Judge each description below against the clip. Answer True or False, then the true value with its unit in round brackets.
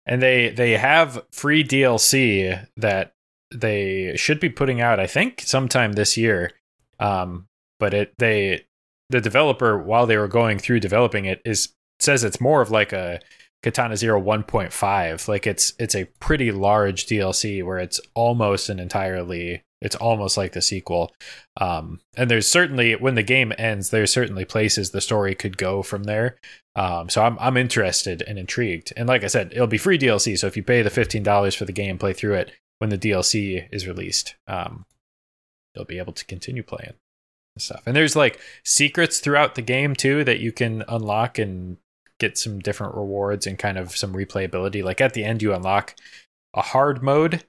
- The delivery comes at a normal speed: True (185 wpm)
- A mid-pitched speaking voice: False (105 Hz)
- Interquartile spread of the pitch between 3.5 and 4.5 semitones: True (3.9 semitones)